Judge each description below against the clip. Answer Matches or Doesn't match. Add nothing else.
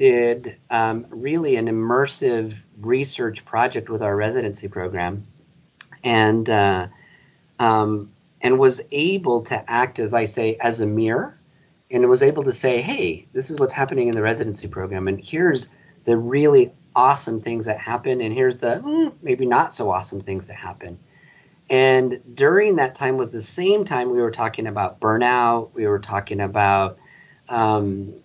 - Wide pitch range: Doesn't match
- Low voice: Matches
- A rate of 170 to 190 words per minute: Doesn't match